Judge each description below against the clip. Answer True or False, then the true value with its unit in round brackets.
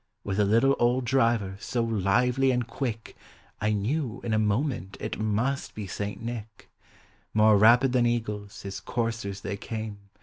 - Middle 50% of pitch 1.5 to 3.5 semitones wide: True (2.8 semitones)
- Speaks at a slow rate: False (160 wpm)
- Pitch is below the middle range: True (110 Hz)